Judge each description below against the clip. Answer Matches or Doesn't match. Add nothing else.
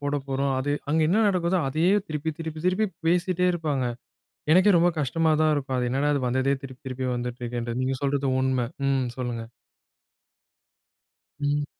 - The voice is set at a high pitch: Doesn't match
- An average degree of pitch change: Matches